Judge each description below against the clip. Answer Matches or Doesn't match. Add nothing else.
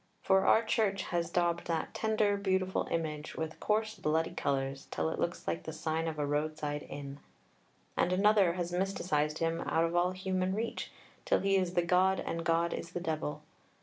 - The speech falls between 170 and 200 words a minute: Matches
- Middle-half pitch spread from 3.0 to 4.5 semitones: Matches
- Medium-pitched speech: Matches